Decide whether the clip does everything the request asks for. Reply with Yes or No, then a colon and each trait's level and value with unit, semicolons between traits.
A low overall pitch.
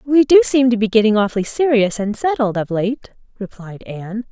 No: high, 225 Hz